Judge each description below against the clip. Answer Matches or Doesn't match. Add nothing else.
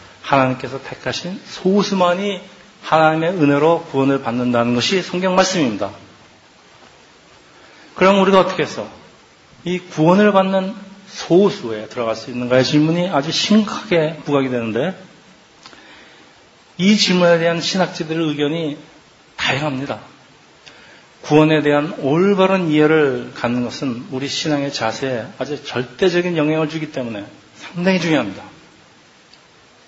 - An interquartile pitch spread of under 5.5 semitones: Matches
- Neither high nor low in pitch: Matches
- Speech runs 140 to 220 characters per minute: Doesn't match